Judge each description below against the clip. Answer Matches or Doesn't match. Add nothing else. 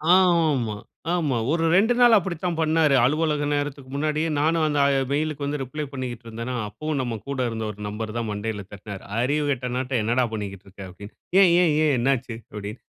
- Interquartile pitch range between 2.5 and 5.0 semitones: Doesn't match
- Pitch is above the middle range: Doesn't match